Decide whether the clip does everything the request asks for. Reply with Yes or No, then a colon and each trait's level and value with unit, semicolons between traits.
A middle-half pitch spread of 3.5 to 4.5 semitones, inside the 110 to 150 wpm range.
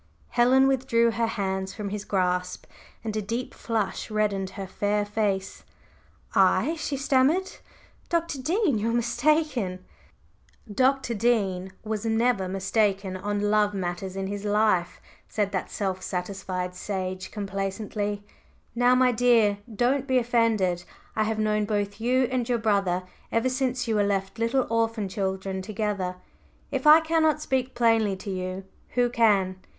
Yes: average, 3.8 semitones; average, 145 wpm